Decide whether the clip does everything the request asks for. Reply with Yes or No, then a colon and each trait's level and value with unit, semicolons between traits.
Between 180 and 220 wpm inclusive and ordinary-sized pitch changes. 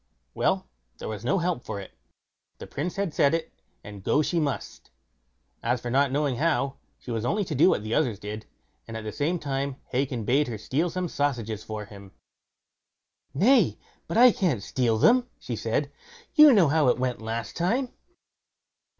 No: average, 185 wpm; wide, 6.9 semitones